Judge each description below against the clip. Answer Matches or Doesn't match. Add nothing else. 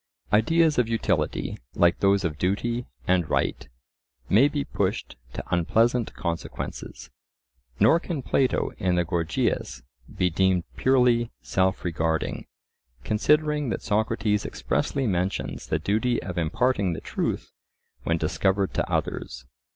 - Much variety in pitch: Matches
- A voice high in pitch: Doesn't match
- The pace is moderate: Doesn't match